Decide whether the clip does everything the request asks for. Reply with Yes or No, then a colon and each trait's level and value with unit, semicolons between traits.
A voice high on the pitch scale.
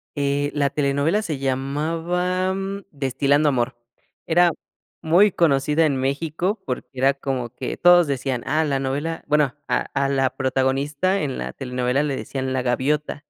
No: medium, 140 Hz